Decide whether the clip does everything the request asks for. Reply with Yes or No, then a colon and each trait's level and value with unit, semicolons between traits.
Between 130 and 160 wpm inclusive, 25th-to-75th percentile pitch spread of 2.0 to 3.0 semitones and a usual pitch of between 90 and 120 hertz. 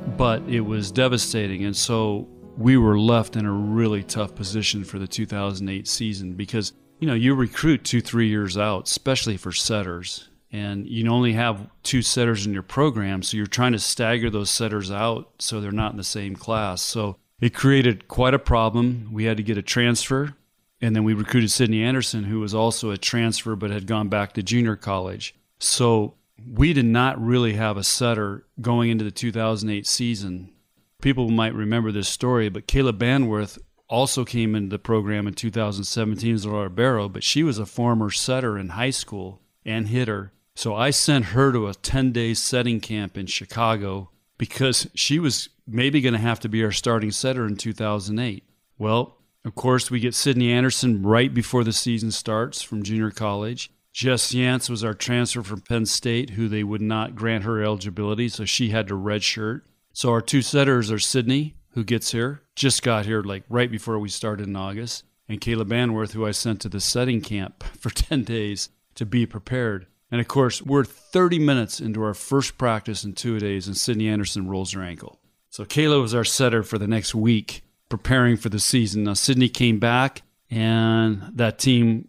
No: average, 190 wpm; average, 2.7 semitones; low, 115 Hz